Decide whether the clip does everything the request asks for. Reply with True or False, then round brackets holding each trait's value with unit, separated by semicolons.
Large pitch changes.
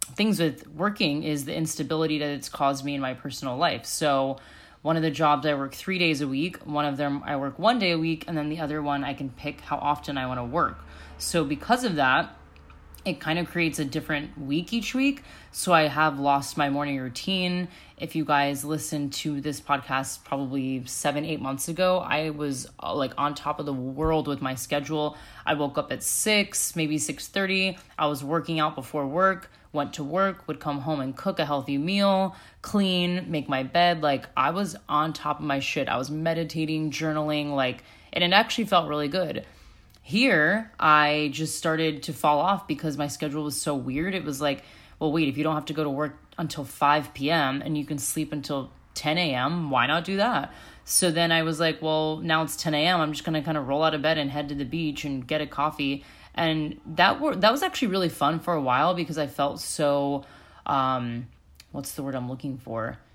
False (2.6 semitones)